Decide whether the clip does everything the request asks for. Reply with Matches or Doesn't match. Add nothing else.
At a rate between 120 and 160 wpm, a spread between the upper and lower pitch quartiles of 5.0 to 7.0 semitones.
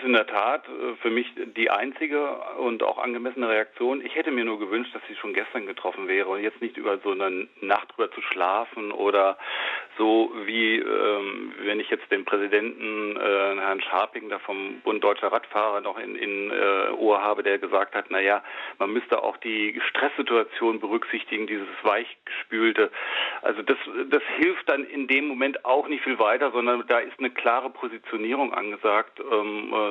Doesn't match